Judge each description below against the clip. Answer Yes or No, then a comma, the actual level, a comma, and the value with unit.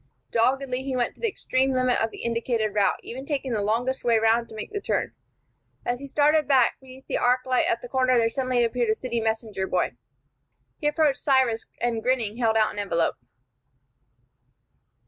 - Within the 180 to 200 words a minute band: Yes, average, 190 wpm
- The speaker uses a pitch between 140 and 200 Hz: No, high, 245 Hz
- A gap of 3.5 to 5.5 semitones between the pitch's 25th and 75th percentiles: No, average, 2.7 semitones